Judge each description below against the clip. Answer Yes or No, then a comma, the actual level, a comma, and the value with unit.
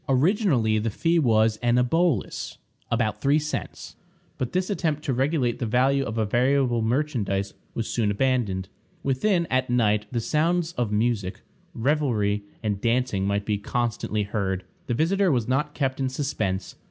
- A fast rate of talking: No, average, 155 wpm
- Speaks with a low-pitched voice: Yes, low, 120 Hz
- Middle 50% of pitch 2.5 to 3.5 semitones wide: No, average, 4.9 semitones